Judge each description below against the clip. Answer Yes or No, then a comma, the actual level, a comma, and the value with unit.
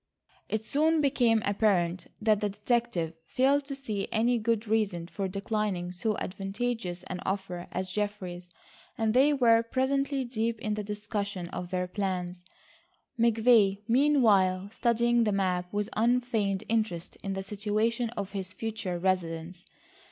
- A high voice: Yes, high, 210 Hz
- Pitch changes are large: No, average, 3.8 semitones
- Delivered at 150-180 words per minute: No, average, 140 wpm